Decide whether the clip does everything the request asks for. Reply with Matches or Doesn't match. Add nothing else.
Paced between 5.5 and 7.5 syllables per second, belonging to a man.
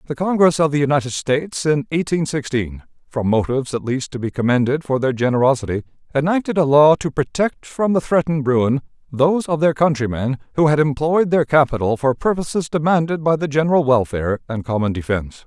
Matches